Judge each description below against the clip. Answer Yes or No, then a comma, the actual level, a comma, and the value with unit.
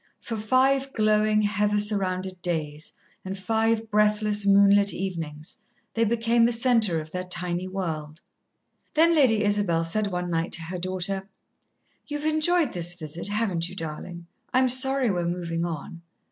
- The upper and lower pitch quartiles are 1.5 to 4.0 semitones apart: No, average, 4.4 semitones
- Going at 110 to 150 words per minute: Yes, average, 145 wpm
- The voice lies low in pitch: No, high, 200 Hz